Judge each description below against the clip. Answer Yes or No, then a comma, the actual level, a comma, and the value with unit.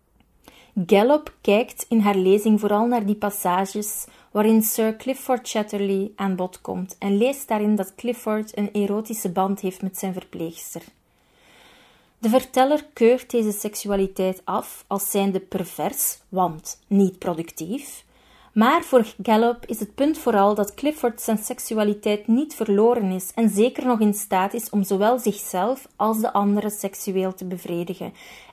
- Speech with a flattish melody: No, average, 3.3 semitones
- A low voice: No, high, 210 Hz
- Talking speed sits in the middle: Yes, average, 145 wpm